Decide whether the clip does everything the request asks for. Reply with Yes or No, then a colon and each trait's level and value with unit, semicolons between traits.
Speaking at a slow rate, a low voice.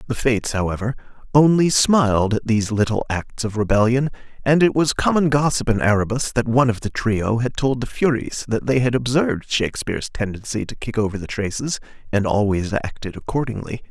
No: average, 180 wpm; low, 115 Hz